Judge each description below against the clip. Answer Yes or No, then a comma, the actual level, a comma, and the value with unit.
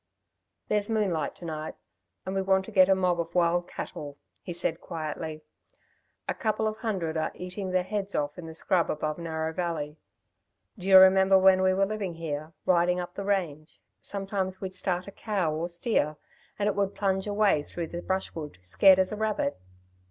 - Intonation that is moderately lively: Yes, average, 3.2 semitones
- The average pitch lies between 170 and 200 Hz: Yes, medium, 185 Hz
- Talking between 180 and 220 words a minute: Yes, average, 190 wpm